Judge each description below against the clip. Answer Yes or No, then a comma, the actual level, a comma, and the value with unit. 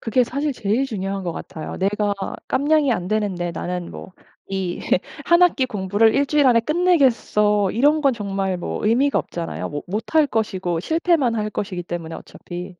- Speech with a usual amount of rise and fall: No, wide, 6.5 semitones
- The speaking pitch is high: Yes, high, 210 Hz